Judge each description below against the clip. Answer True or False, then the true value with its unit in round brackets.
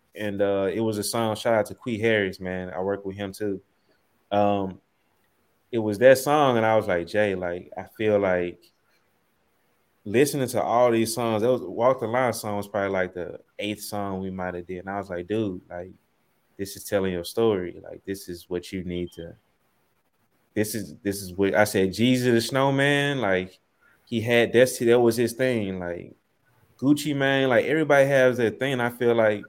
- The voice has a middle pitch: False (105 Hz)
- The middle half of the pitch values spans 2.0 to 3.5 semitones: False (4.1 semitones)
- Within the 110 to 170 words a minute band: False (200 wpm)